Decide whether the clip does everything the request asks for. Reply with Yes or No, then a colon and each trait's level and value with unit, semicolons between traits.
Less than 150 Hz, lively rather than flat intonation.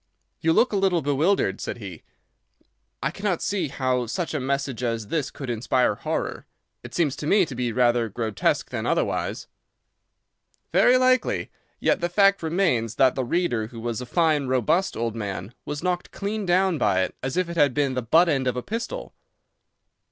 Yes: medium, 140 Hz; wide, 6.7 semitones